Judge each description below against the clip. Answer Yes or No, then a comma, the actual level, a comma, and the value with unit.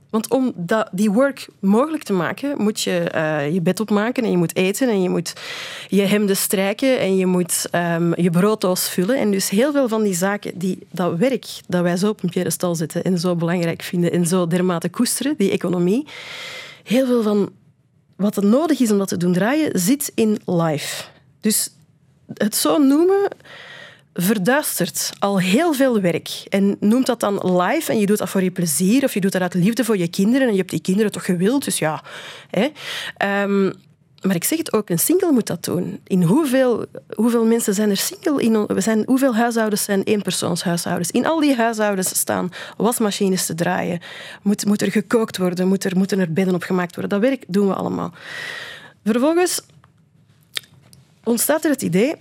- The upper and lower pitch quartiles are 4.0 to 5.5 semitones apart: Yes, average, 4.5 semitones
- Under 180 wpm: No, average, 190 wpm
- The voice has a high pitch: Yes, high, 200 Hz